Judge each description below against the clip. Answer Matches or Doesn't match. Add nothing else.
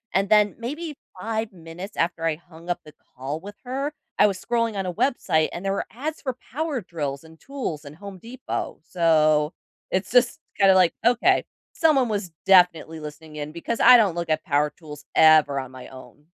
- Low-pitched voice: Doesn't match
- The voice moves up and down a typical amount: Doesn't match